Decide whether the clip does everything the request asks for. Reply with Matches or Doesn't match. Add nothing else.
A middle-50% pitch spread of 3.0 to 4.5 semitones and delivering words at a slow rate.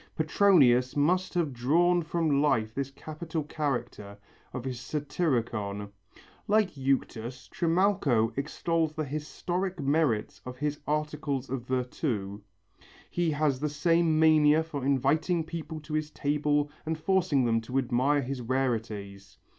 Matches